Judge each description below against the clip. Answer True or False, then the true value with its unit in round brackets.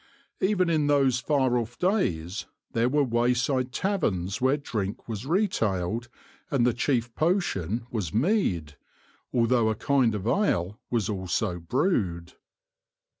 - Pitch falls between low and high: False (120 Hz)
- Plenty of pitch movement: True (6.2 semitones)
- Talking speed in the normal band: False (125 wpm)